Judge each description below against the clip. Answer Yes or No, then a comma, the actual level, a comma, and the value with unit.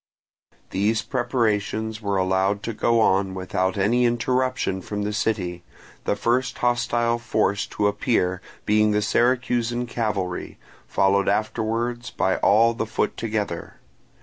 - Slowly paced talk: Yes, slow, 125 wpm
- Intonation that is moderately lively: Yes, average, 3.0 semitones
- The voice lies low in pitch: Yes, low, 110 Hz